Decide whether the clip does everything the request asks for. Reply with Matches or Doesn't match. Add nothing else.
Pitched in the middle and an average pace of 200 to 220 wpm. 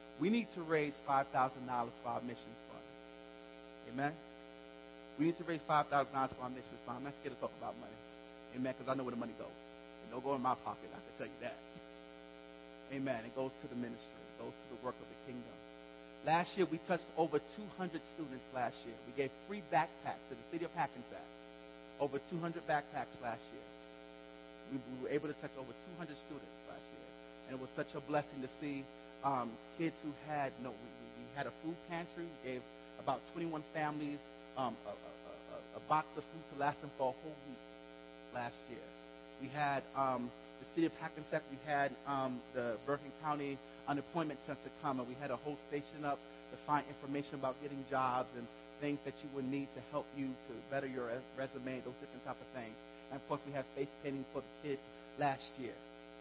Doesn't match